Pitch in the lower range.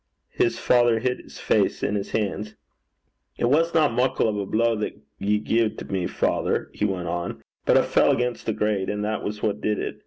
Yes: low, 110 Hz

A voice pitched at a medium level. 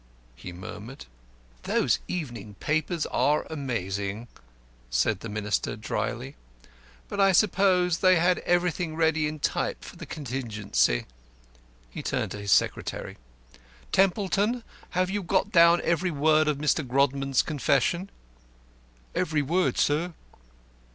Yes: medium, 155 Hz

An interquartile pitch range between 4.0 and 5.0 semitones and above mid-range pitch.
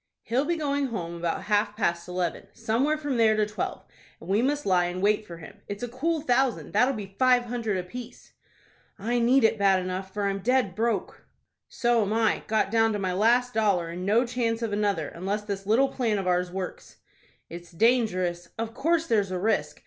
Yes: average, 4.4 semitones; high, 215 Hz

